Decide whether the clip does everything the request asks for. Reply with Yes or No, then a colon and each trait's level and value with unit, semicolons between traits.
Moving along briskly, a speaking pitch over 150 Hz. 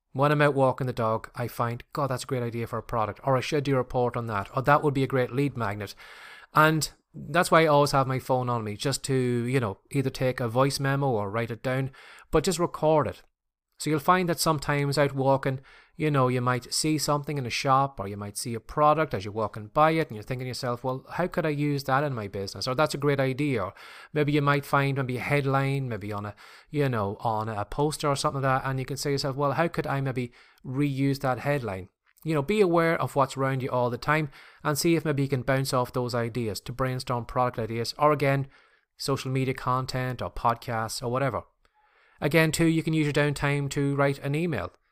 No: fast, 245 wpm; low, 135 Hz